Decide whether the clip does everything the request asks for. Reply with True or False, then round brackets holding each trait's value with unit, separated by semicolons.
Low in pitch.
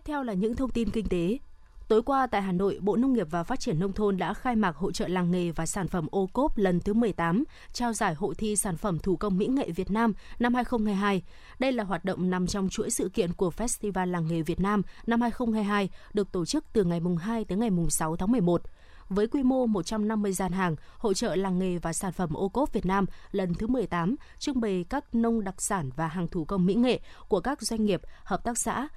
False (205 Hz)